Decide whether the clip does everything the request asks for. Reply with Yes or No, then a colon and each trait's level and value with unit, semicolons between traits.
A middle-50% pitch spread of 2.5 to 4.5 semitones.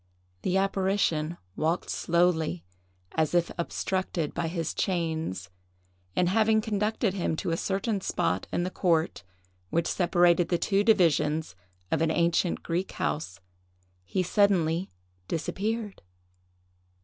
Yes: average, 3.1 semitones